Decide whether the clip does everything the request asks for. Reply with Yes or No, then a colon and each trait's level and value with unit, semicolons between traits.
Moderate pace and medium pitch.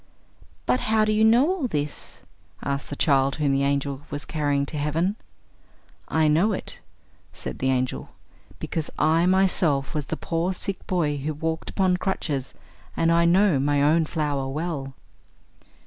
Yes: average, 160 wpm; medium, 155 Hz